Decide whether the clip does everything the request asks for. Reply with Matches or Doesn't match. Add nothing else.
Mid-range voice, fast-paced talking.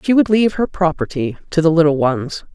Matches